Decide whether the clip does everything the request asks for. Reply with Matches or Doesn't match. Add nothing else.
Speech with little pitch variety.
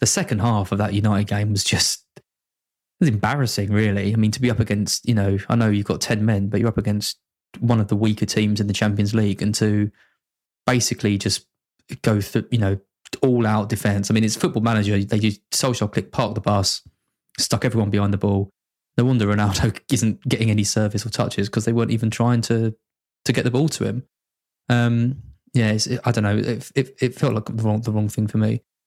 Matches